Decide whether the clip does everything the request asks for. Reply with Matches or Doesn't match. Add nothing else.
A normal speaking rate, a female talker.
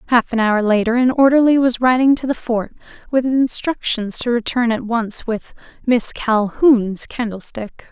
Matches